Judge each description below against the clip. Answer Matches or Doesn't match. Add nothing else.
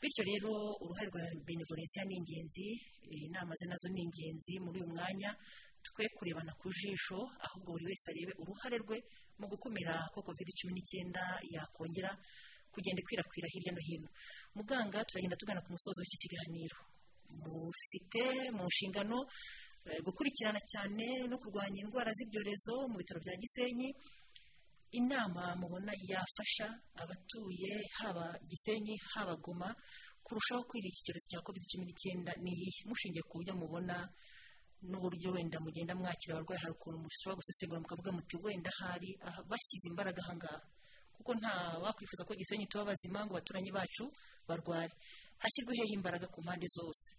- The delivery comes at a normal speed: Doesn't match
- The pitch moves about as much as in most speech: Matches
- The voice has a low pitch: Doesn't match